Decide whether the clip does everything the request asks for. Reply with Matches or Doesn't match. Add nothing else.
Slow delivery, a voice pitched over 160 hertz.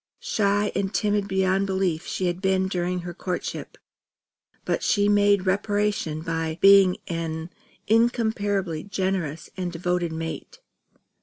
Matches